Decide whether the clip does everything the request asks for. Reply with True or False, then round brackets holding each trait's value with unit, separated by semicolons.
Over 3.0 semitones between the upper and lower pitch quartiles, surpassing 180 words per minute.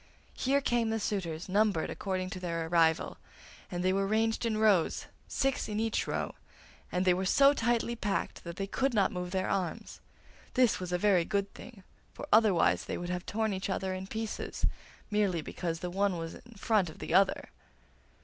True (3.6 semitones; 190 wpm)